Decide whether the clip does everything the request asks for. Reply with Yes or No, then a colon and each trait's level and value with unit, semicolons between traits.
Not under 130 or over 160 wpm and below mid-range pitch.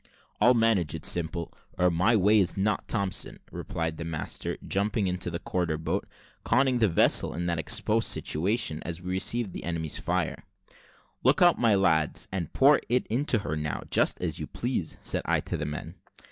No: average, 185 wpm; very low, 90 Hz